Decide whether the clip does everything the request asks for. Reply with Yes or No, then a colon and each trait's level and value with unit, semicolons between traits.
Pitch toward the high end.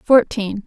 Yes: high, 215 Hz